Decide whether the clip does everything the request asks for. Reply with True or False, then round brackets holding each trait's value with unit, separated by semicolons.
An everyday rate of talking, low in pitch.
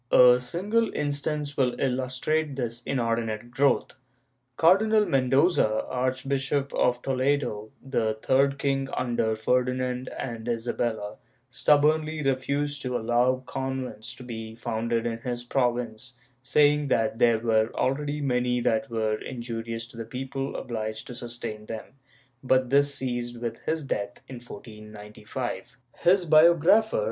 False (130 wpm; 125 Hz)